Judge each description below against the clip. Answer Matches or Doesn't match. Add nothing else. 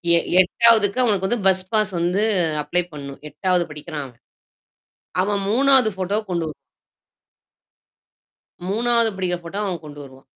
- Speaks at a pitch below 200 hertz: Matches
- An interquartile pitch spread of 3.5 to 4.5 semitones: Matches